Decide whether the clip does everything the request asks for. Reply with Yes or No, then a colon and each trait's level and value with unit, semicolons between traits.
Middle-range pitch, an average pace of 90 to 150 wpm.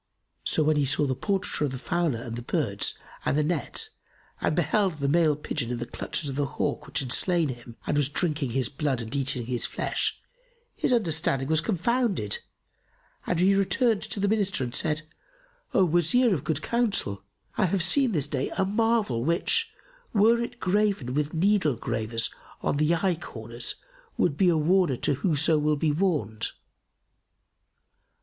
No: medium, 155 Hz; average, 175 wpm